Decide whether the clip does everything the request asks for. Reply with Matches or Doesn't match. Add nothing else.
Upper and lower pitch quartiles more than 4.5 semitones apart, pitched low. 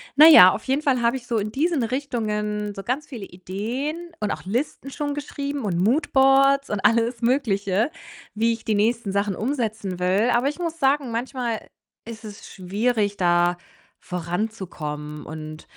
Doesn't match